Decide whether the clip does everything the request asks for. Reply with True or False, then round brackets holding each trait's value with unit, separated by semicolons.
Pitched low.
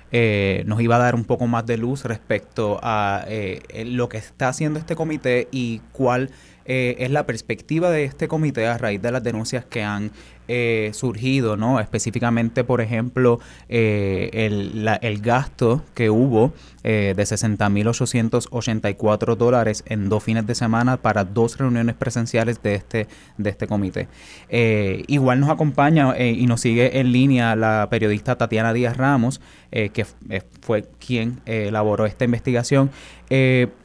True (115 Hz)